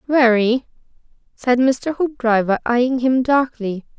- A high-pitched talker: Yes, high, 245 Hz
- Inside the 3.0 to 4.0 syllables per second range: Yes, 3.7 syllables/s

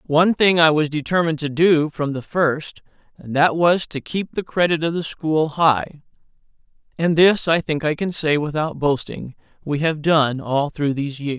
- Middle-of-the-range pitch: Yes, medium, 155 Hz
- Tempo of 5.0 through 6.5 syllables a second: No, 4.7 syllables/s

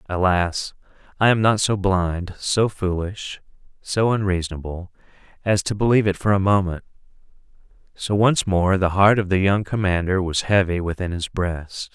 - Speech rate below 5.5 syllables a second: Yes, 4.8 syllables/s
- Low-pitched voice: Yes, very low, 95 Hz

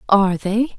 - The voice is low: No, high, 205 Hz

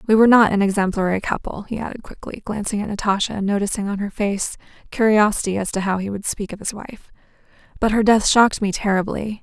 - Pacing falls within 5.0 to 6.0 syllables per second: No, 6.2 syllables/s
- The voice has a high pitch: Yes, high, 205 Hz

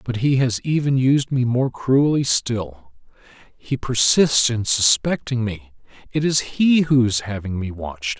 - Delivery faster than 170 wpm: No, average, 160 wpm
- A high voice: No, low, 120 Hz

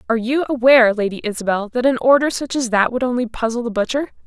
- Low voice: No, high, 240 Hz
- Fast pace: Yes, fast, 225 wpm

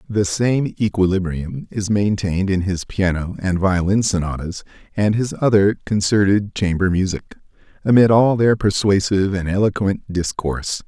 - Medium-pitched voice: No, low, 100 Hz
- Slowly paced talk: Yes, slow, 130 wpm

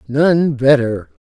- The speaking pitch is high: No, medium, 140 Hz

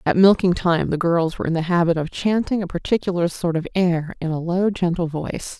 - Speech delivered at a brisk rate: Yes, fast, 225 wpm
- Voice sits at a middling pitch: Yes, medium, 175 Hz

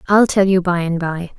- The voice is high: No, medium, 180 Hz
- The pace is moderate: No, fast, 260 wpm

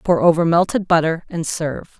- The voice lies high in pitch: No, medium, 165 Hz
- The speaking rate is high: No, average, 180 wpm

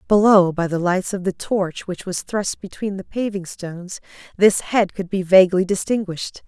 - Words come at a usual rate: Yes, average, 185 wpm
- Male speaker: No, female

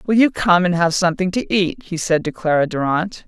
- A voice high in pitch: No, medium, 180 Hz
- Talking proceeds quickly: Yes, fast, 240 wpm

